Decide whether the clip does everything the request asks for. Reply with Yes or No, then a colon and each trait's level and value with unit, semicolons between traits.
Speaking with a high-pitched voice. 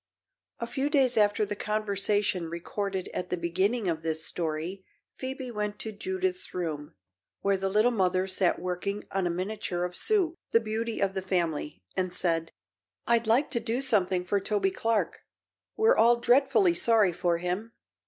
Yes: high, 200 Hz